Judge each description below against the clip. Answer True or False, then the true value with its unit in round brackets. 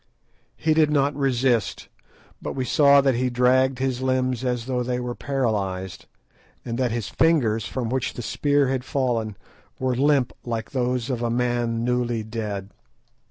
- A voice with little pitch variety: True (2.2 semitones)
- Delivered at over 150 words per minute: True (160 wpm)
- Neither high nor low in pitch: False (125 Hz)